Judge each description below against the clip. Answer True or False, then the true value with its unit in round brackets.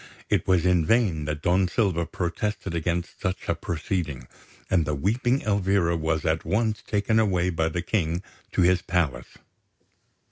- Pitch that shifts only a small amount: False (3.6 semitones)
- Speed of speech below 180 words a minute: True (155 wpm)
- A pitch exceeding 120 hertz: False (90 Hz)